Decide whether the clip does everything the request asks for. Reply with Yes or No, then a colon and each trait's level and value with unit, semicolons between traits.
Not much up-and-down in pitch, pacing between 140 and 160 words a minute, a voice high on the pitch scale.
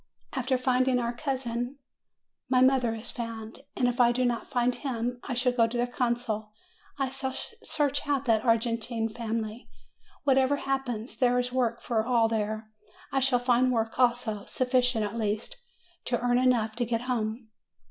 No: narrow, 2.0 semitones; average, 170 wpm; high, 245 Hz